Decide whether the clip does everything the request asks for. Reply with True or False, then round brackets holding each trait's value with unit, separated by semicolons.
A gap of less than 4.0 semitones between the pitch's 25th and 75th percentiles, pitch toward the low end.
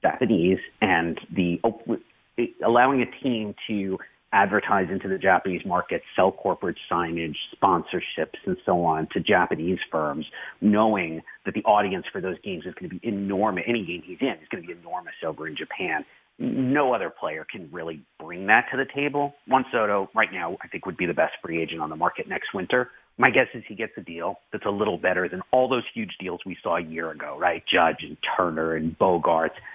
False (5.3 semitones; 100 Hz)